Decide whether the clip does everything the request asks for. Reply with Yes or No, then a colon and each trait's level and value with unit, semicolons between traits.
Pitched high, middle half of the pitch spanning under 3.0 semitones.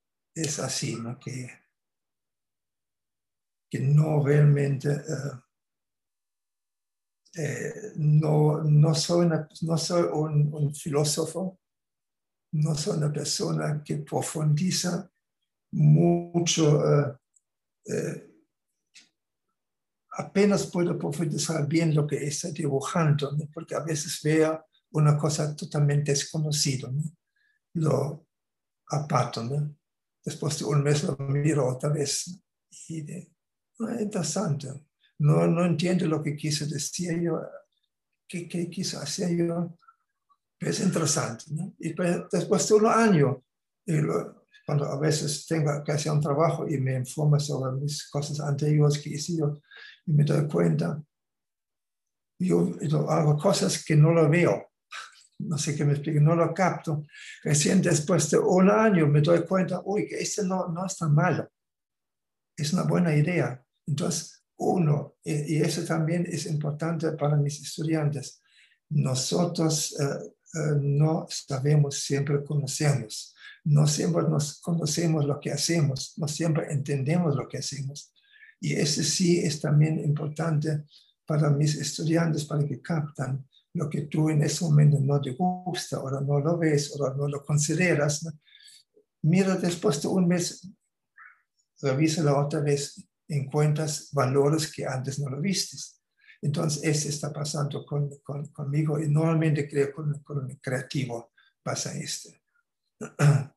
No: medium, 155 Hz; narrow, 2.6 semitones